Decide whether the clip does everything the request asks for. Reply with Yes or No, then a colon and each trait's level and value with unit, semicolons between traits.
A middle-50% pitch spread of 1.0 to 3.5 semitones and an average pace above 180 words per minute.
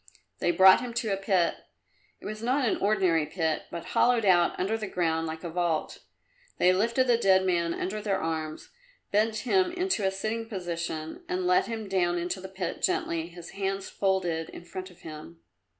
No: average, 4.3 semitones; average, 190 wpm